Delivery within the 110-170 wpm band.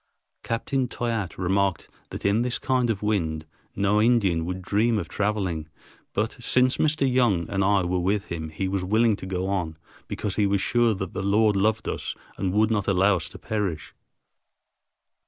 No: average, 180 wpm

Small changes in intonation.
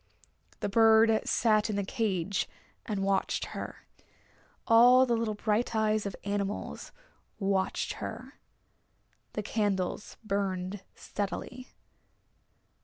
Yes: narrow, 2.1 semitones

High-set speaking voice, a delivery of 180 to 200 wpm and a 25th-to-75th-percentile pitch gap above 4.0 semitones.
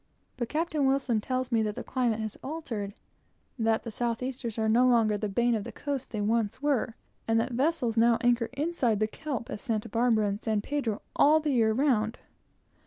No: high, 235 Hz; average, 195 wpm; average, 3.3 semitones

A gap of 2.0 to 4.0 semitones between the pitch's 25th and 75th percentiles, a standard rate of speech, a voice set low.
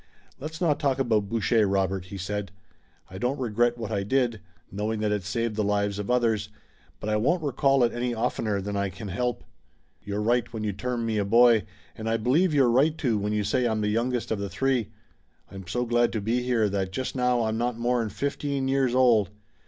No: average, 3.3 semitones; fast, 215 wpm; low, 115 Hz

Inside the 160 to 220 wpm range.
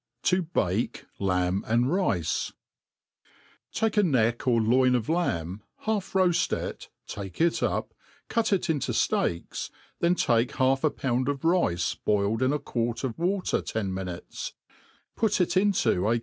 No: average, 150 wpm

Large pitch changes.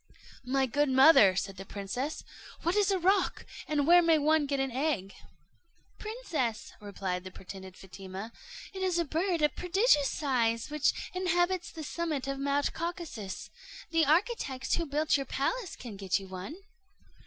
Yes: wide, 7.2 semitones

